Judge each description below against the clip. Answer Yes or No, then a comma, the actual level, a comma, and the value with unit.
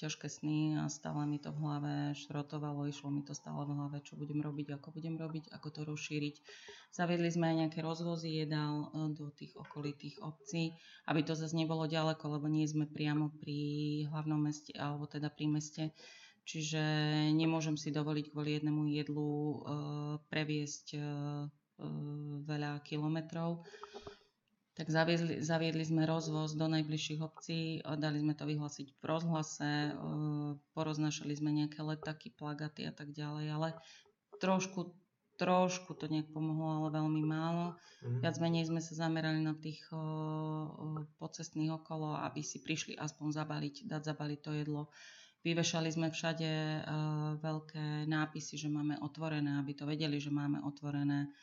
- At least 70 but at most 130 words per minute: No, average, 145 wpm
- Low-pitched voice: No, medium, 155 Hz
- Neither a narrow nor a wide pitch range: No, narrow, 1.2 semitones